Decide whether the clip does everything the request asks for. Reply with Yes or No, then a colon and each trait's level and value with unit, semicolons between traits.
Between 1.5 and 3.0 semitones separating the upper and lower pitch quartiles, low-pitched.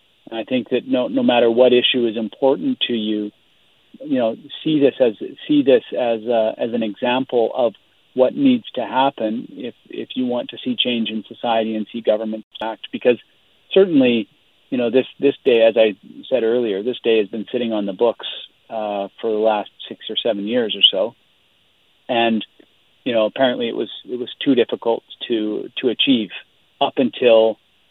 Yes: narrow, 2.5 semitones; low, 115 Hz